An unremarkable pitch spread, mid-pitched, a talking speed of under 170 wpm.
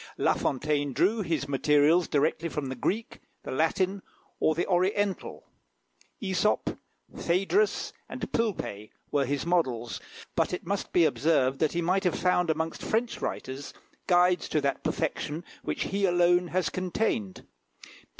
Yes: average, 4.4 semitones; medium, 170 Hz; average, 140 wpm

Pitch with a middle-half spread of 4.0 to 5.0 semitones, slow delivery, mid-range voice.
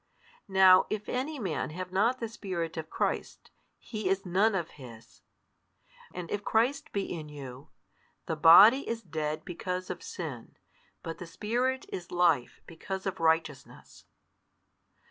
No: average, 4.6 semitones; average, 145 wpm; medium, 180 Hz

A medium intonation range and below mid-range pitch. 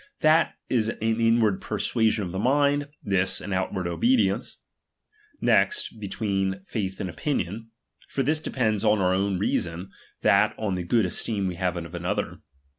Yes: average, 3.5 semitones; low, 100 Hz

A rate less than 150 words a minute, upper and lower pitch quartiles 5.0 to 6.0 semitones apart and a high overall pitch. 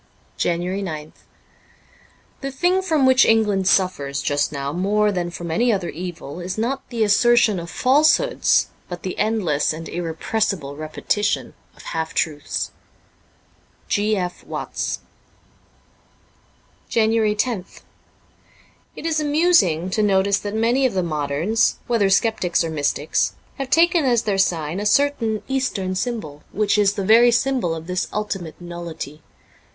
Yes: average, 140 wpm; wide, 5.4 semitones; high, 200 Hz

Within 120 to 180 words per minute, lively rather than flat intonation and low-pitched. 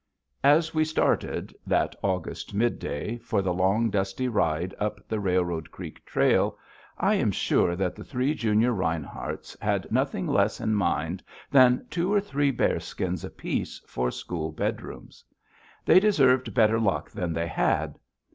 Yes: average, 145 wpm; wide, 6.2 semitones; low, 105 Hz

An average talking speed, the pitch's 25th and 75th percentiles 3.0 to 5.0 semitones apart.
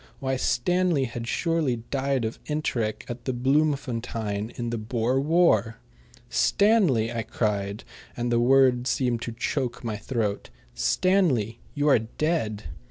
No: slow, 130 wpm; average, 3.7 semitones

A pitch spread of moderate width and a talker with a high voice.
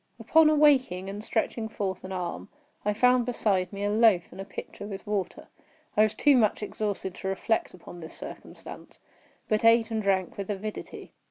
Yes: average, 3.0 semitones; high, 210 Hz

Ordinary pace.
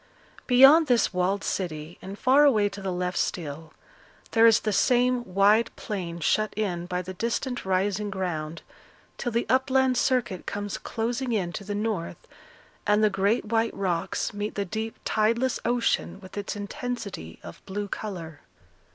Yes: average, 160 wpm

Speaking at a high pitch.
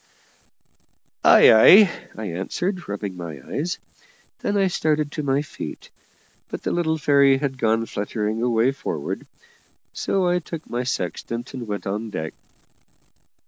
No: low, 130 Hz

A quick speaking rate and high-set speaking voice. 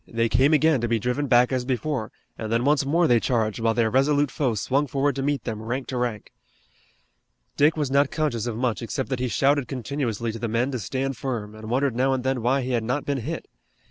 No: fast, 235 wpm; low, 125 Hz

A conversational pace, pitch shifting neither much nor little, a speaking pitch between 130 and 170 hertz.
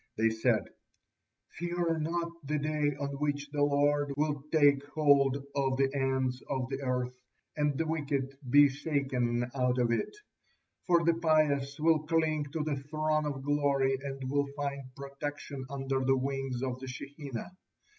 No: average, 155 wpm; narrow, 2.0 semitones; medium, 140 Hz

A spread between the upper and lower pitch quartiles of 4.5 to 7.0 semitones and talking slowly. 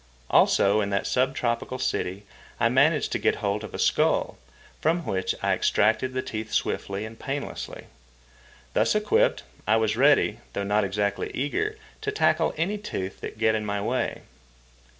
No: average, 5.2 semitones; average, 165 wpm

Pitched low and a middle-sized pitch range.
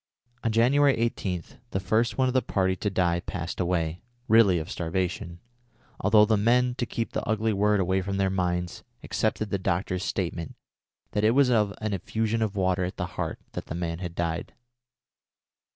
Yes: very low, 95 Hz; average, 3.7 semitones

